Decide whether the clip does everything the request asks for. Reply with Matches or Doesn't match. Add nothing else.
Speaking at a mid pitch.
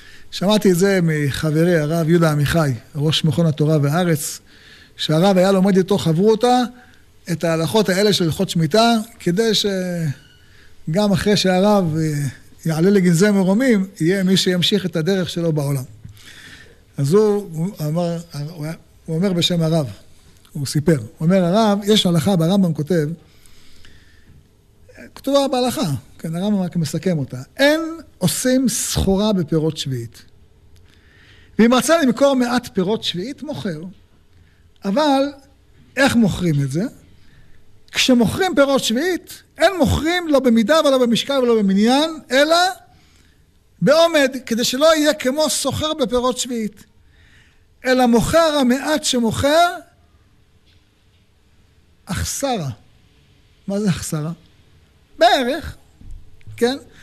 Matches